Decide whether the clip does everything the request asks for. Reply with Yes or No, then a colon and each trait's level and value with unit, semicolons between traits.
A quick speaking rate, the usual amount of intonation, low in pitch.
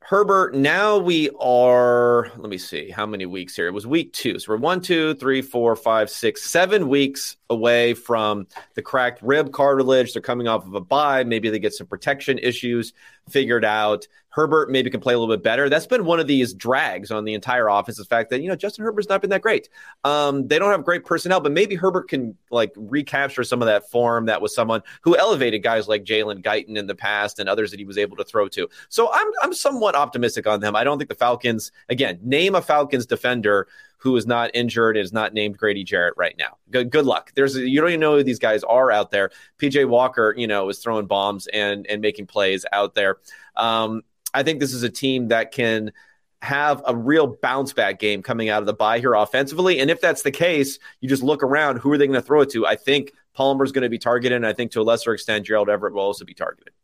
Yes: fast, 240 wpm; average, 4.8 semitones; low, 125 Hz